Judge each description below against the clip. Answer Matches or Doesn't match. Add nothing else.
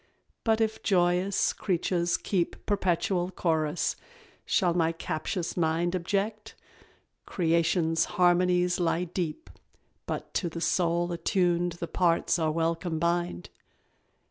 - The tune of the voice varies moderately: Doesn't match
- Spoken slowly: Matches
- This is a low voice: Doesn't match